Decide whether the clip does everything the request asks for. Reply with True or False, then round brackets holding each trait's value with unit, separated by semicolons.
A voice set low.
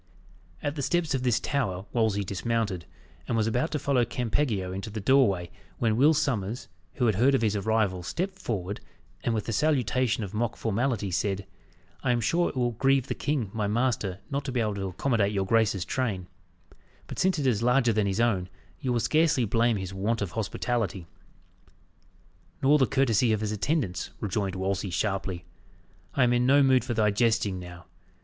True (115 Hz)